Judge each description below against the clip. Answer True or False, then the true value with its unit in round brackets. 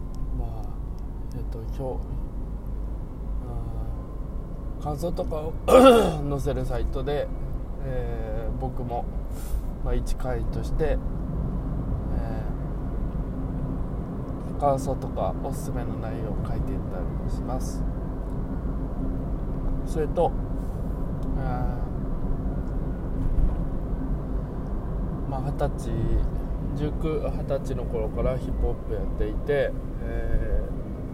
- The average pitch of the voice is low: True (130 Hz)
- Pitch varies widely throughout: False (3.8 semitones)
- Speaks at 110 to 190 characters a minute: True (165 characters per minute)